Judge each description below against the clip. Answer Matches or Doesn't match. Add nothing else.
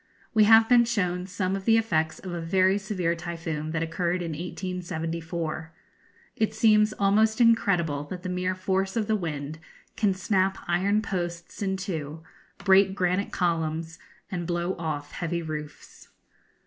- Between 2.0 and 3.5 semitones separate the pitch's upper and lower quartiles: Matches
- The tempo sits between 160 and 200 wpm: Doesn't match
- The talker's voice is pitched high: Doesn't match